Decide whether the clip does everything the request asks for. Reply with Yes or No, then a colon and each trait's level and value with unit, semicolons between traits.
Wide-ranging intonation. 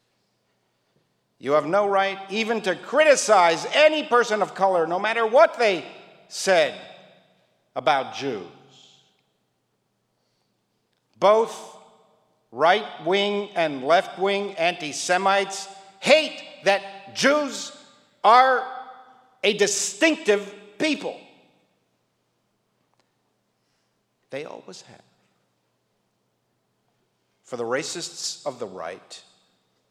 Yes: wide, 6.4 semitones